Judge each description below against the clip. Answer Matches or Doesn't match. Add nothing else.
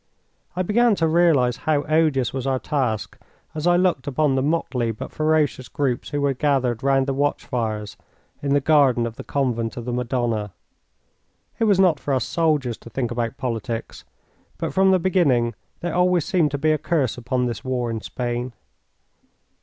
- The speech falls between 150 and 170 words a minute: Doesn't match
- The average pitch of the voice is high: Doesn't match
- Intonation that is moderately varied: Matches